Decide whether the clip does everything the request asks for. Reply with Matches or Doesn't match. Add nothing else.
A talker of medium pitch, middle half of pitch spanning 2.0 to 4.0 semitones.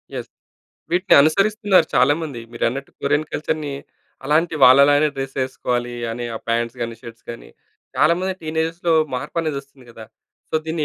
Doesn't match